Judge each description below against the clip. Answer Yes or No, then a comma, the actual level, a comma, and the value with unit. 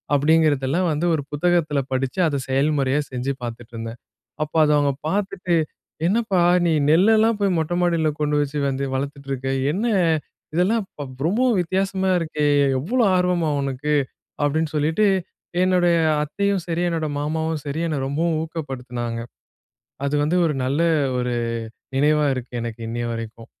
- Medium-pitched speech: Yes, medium, 150 Hz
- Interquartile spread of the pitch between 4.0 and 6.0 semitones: Yes, average, 4.4 semitones